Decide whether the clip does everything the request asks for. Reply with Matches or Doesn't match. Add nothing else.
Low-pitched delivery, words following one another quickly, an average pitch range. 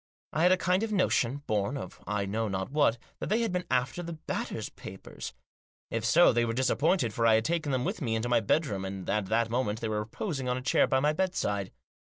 Doesn't match